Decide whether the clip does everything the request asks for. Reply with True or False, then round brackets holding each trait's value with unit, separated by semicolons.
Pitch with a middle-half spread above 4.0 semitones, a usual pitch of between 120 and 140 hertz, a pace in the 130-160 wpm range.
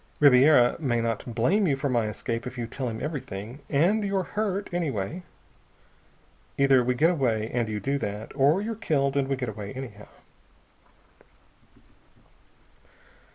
True (5.0 semitones; 135 Hz; 150 wpm)